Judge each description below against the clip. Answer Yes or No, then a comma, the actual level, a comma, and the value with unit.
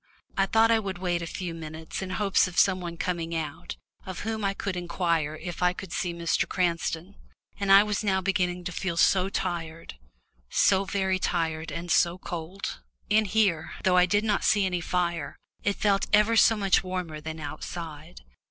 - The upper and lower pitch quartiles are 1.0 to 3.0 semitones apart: Yes, average, 2.7 semitones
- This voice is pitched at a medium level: Yes, medium, 180 Hz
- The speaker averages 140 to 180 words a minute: No, average, 190 wpm